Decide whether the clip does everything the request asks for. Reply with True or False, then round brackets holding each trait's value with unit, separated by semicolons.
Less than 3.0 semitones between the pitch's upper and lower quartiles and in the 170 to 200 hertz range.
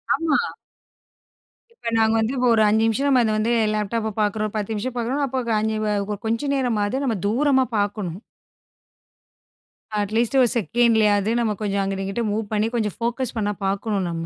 False (2.5 semitones; 220 Hz)